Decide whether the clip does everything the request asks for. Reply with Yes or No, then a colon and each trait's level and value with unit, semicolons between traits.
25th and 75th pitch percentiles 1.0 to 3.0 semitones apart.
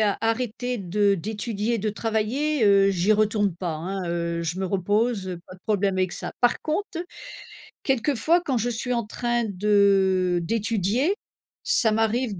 No: average, 3.7 semitones